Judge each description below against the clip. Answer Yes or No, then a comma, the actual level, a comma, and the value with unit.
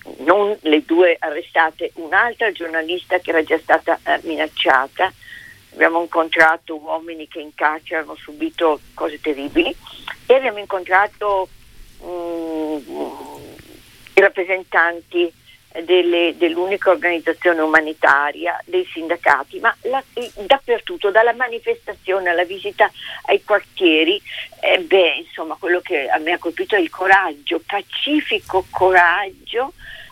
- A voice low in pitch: No, medium, 180 Hz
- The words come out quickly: No, slow, 115 wpm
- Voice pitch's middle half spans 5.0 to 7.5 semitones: No, average, 4.3 semitones